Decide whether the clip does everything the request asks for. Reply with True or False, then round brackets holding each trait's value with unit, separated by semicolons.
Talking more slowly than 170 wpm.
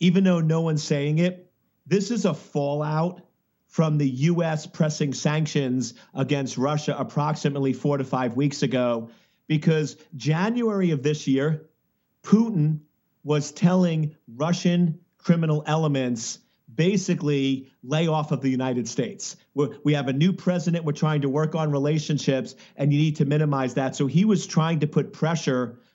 True (155 wpm)